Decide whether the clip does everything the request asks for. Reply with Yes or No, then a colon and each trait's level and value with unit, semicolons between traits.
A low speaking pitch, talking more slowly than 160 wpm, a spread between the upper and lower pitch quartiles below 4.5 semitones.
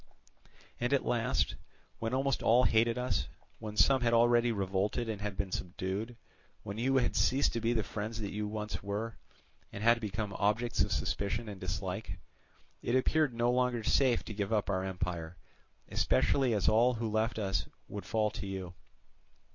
No: low, 110 Hz; average, 175 wpm; average, 3.0 semitones